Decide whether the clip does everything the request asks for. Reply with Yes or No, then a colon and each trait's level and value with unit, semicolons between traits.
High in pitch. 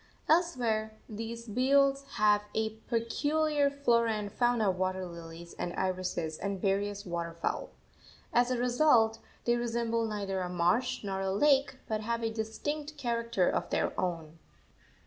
Yes: high, 220 Hz